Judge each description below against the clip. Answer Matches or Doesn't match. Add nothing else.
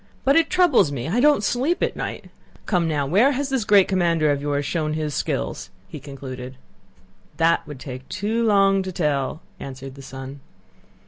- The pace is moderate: Matches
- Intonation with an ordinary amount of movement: Doesn't match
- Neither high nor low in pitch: Matches